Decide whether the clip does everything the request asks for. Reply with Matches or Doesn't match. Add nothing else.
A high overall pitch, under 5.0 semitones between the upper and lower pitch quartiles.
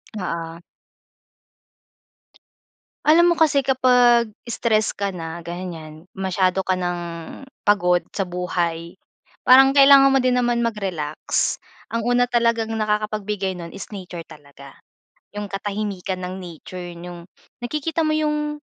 Doesn't match